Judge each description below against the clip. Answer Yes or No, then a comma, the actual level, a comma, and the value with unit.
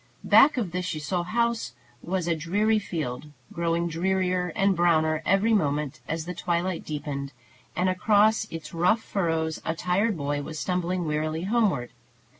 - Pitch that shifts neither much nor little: Yes, average, 3.4 semitones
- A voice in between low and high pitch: Yes, medium, 175 Hz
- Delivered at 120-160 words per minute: Yes, average, 150 wpm